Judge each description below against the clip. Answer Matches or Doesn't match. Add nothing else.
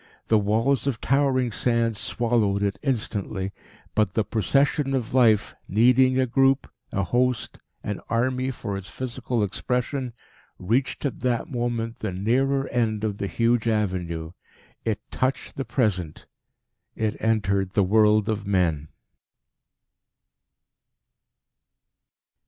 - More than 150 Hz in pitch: Doesn't match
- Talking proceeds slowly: Matches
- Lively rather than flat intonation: Doesn't match